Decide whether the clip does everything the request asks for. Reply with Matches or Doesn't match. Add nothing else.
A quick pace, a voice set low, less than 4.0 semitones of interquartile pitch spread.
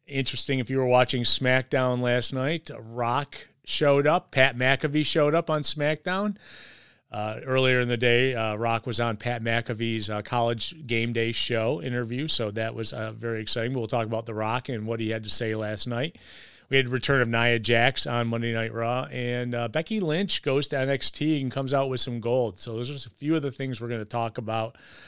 Matches